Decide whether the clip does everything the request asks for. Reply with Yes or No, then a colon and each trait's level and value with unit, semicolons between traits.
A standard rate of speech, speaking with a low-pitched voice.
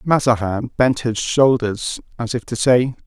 Yes: average, 155 wpm; low, 120 Hz